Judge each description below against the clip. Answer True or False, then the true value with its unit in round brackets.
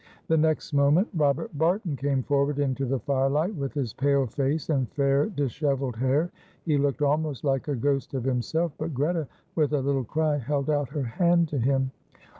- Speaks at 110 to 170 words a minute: False (185 wpm)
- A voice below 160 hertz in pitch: True (140 Hz)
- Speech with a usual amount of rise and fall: False (2.3 semitones)